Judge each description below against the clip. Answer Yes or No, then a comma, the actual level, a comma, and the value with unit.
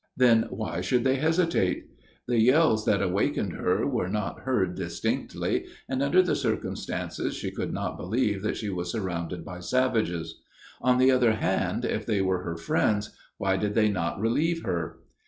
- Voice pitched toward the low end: Yes, low, 105 Hz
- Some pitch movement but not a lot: No, wide, 5.7 semitones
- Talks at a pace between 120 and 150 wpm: No, average, 170 wpm